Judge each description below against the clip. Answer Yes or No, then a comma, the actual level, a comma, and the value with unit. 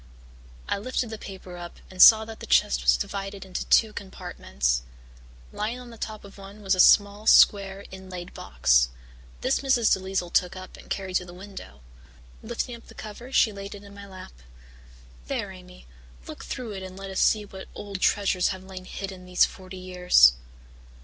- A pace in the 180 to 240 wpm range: Yes, average, 190 wpm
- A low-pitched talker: No, high, 195 Hz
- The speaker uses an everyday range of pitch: No, narrow, 2.1 semitones